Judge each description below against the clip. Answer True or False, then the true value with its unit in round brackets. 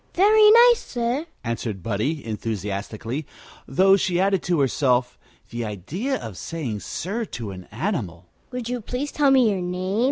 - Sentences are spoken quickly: False (155 wpm)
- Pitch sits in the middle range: True (170 Hz)